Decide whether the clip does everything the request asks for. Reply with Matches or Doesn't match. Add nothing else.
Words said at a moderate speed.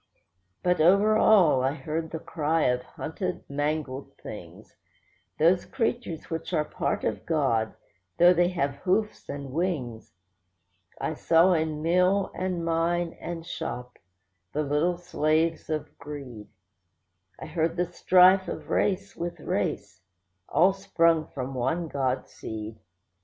Doesn't match